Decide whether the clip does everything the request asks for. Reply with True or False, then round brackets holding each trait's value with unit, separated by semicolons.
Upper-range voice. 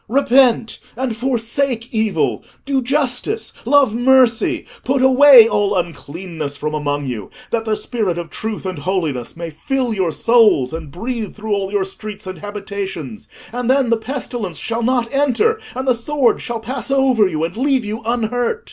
True (225 Hz)